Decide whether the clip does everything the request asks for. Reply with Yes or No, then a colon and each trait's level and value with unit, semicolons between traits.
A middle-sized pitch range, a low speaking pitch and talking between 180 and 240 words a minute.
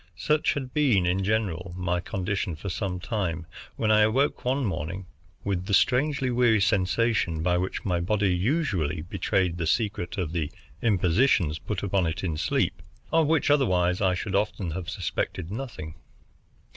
No: average, 4.2 semitones; very low, 95 Hz; average, 160 wpm